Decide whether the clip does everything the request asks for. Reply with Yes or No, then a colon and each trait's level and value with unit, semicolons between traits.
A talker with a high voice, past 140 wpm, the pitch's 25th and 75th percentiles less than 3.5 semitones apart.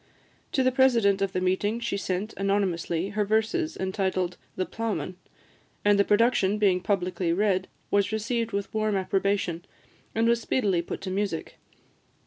Yes: high, 200 Hz; average, 150 wpm; average, 2.7 semitones